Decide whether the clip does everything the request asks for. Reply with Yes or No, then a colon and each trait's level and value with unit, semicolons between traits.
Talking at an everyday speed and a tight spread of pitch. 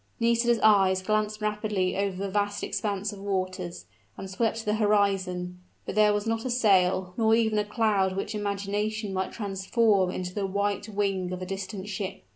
Yes: average, 175 wpm; narrow, 2.0 semitones